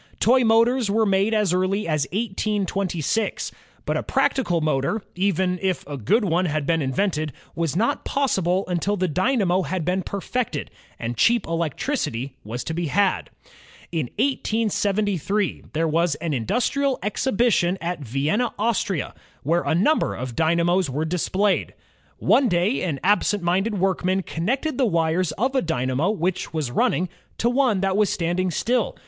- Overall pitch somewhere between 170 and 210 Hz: Yes, medium, 185 Hz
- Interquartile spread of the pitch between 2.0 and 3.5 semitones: No, average, 4.6 semitones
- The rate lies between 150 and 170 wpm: Yes, average, 155 wpm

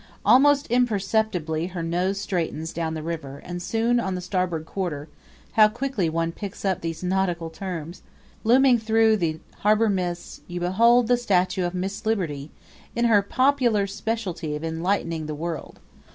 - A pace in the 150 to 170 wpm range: Yes, average, 155 wpm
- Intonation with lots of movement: No, average, 5.0 semitones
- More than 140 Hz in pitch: Yes, medium, 185 Hz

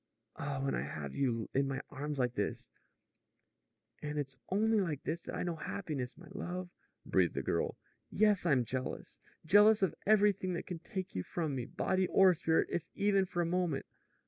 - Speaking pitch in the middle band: Yes, medium, 165 Hz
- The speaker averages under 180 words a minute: No, average, 190 wpm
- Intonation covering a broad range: Yes, wide, 5.7 semitones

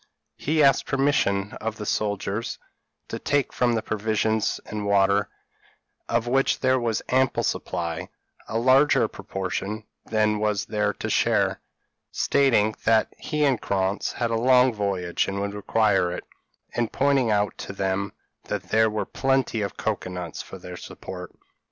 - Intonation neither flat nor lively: Yes, average, 3.7 semitones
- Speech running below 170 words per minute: Yes, average, 150 wpm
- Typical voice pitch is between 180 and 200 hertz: No, low, 110 Hz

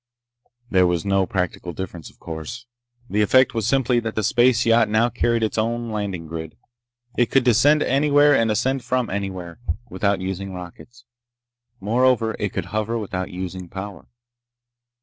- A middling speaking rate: Yes, average, 155 wpm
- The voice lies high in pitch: No, low, 110 Hz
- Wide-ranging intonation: No, average, 4.3 semitones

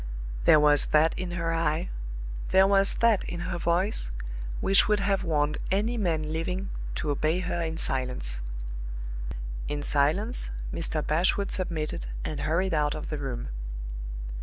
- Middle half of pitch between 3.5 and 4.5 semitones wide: Yes, average, 4.0 semitones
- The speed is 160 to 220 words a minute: No, average, 145 wpm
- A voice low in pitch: No, medium, 165 Hz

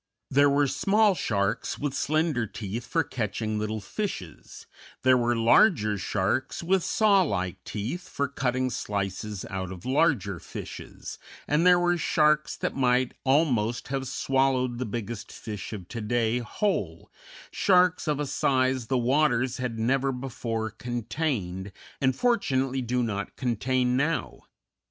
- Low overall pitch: Yes, low, 125 Hz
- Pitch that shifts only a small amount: No, average, 4.6 semitones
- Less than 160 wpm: Yes, average, 140 wpm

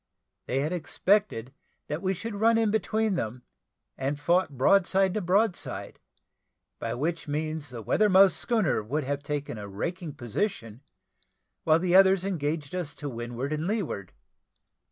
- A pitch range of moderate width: No, wide, 6.0 semitones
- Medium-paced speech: Yes, average, 155 wpm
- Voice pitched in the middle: Yes, medium, 160 Hz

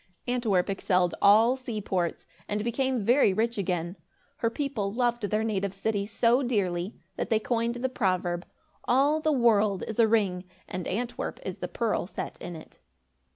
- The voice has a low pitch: No, high, 215 Hz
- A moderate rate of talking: Yes, average, 160 wpm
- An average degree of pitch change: Yes, average, 3.9 semitones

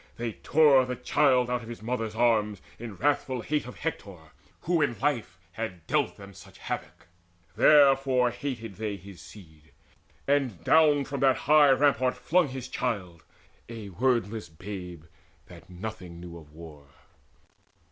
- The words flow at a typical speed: Yes, average, 150 wpm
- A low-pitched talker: Yes, low, 115 Hz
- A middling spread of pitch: No, wide, 6.3 semitones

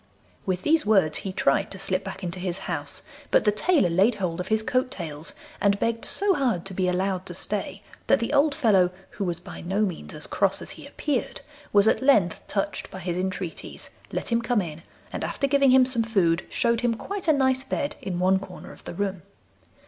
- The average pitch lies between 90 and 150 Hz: No, high, 195 Hz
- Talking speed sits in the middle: No, fast, 215 wpm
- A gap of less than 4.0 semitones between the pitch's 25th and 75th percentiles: No, average, 5.1 semitones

